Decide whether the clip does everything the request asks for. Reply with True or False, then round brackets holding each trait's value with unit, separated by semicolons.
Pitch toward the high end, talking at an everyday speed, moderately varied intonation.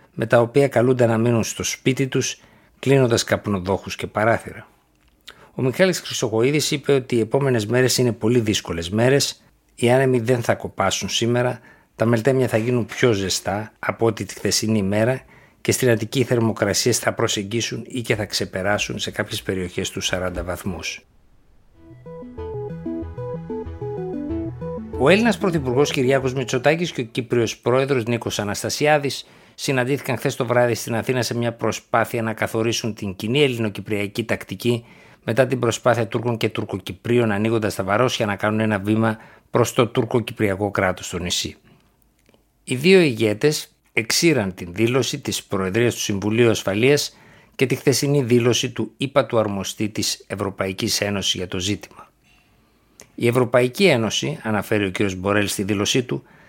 False (115 Hz; 150 wpm; 3.8 semitones)